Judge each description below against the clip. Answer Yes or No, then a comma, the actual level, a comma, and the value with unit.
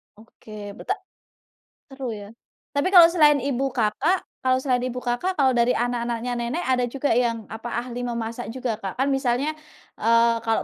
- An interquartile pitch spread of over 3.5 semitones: No, average, 2.8 semitones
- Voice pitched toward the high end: Yes, high, 245 Hz